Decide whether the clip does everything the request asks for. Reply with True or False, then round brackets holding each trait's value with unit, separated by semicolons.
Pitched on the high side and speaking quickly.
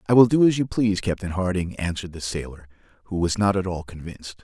False (95 Hz; 230 wpm)